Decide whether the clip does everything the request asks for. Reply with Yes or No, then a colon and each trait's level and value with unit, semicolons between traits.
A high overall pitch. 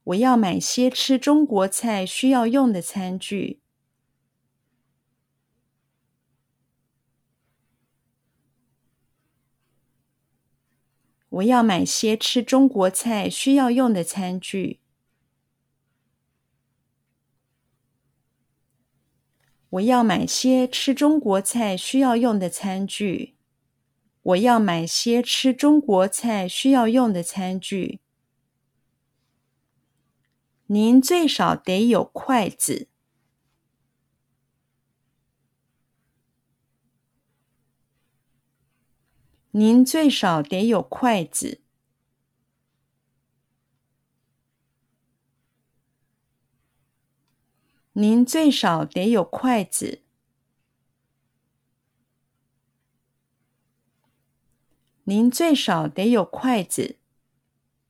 No: low, 135 Hz